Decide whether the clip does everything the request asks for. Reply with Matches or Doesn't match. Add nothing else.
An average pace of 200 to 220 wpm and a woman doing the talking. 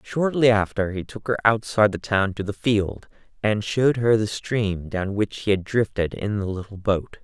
Doesn't match